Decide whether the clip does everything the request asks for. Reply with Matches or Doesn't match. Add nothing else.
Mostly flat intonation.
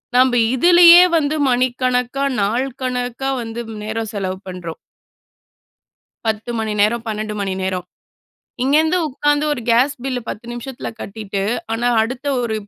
Doesn't match